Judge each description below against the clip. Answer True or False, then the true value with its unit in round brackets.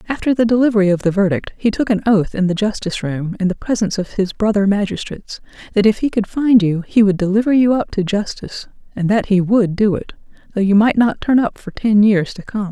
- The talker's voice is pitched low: False (205 Hz)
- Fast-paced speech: True (240 wpm)